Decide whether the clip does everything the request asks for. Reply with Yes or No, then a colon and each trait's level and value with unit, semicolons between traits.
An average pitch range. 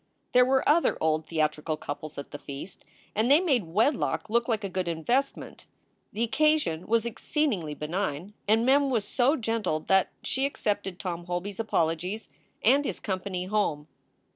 No: wide, 6.6 semitones